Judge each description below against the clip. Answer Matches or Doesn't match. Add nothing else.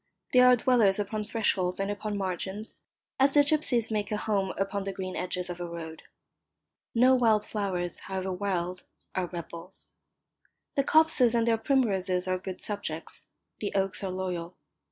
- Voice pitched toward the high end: Matches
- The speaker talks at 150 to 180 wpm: Matches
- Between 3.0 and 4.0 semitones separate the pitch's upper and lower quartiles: Matches